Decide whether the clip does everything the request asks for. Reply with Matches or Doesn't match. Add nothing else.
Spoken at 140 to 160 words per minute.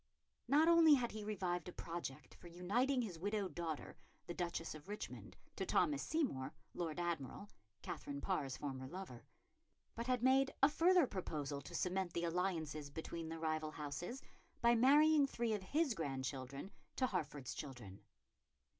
Matches